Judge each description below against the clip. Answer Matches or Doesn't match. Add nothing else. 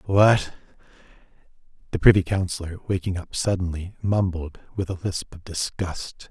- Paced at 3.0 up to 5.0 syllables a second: Matches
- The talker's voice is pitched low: Matches